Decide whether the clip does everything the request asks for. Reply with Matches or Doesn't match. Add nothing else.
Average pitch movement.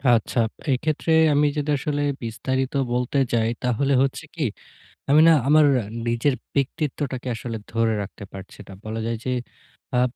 Matches